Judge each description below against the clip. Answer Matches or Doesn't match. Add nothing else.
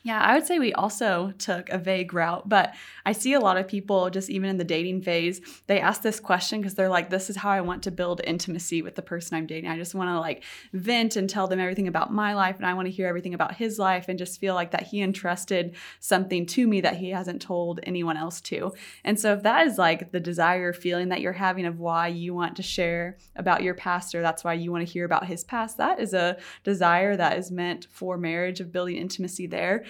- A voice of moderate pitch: Matches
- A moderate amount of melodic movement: Doesn't match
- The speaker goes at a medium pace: Doesn't match